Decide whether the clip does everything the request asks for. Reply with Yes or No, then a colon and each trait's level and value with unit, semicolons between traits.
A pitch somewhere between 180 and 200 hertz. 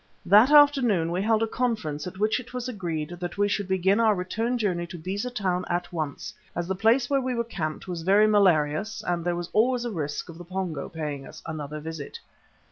Yes: high, 190 Hz